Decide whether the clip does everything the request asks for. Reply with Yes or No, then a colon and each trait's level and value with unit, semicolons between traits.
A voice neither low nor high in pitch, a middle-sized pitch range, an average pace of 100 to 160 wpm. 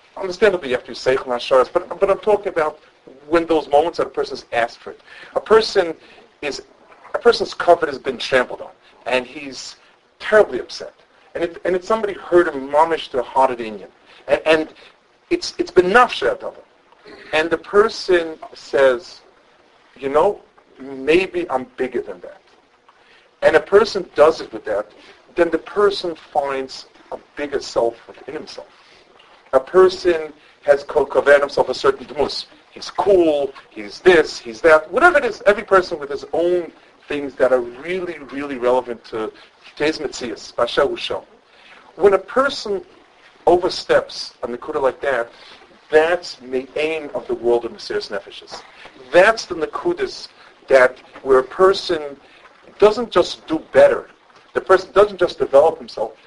No: medium, 175 Hz; wide, 6.6 semitones; average, 155 wpm